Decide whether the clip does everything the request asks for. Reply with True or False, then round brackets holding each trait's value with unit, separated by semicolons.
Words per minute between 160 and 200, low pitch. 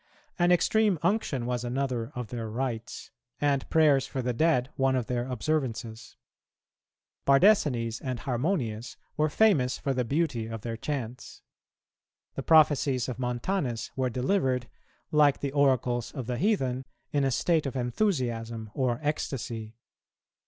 False (140 wpm; 130 Hz)